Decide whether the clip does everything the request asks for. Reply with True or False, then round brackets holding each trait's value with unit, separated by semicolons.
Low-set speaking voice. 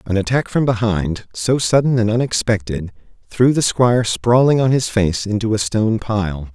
True (115 Hz)